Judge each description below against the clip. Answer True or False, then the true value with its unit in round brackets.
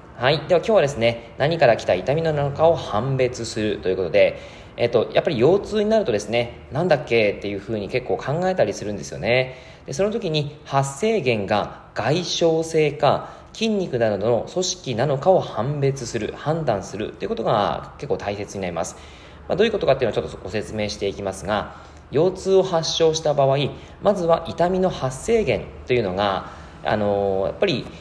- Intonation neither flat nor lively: False (7.5 semitones)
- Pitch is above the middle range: False (135 Hz)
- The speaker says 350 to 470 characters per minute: True (380 characters per minute)